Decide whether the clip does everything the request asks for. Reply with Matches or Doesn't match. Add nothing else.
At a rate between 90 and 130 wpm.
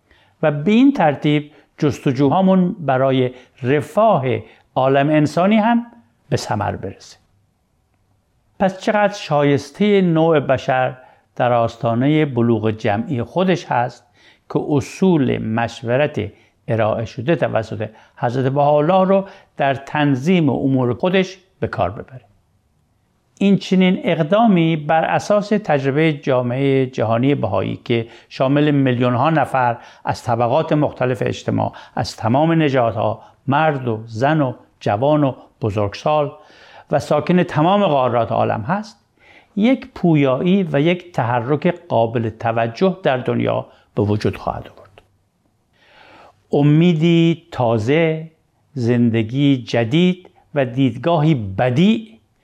Matches